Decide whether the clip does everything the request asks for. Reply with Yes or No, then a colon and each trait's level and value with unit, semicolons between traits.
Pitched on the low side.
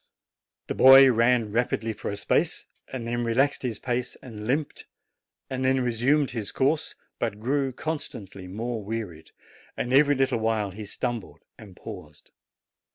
Yes: low, 120 Hz